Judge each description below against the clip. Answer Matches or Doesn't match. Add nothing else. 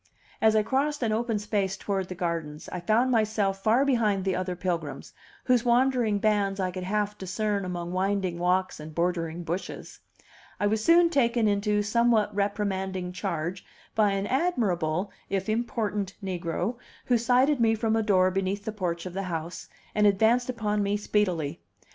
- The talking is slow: Doesn't match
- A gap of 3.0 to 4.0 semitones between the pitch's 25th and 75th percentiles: Matches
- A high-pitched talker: Matches